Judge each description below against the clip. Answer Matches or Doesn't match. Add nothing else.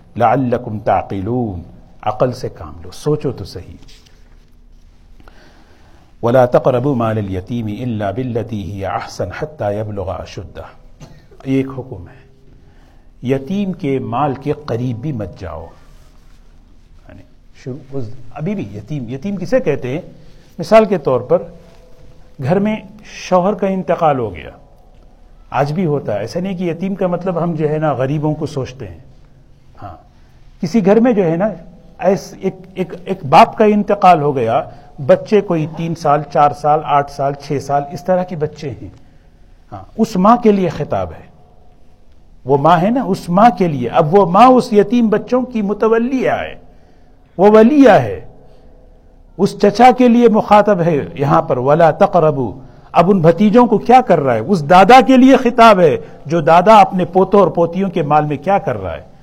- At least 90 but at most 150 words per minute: Doesn't match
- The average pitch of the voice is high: Doesn't match